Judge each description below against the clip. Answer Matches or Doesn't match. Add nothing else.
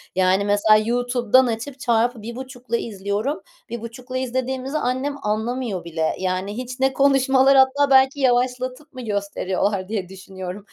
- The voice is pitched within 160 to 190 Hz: Doesn't match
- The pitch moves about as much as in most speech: Matches